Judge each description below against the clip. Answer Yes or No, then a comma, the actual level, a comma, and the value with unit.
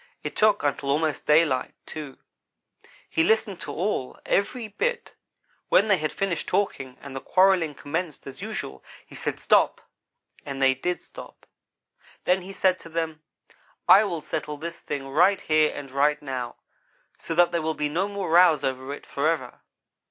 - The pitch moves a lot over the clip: No, average, 4.7 semitones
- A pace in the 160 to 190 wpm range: Yes, average, 170 wpm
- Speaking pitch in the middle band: Yes, medium, 160 Hz